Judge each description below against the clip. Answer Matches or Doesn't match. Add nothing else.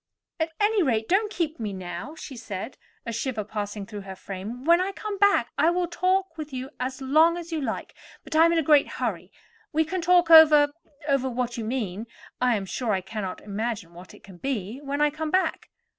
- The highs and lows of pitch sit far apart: Matches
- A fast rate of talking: Matches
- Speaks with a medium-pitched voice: Doesn't match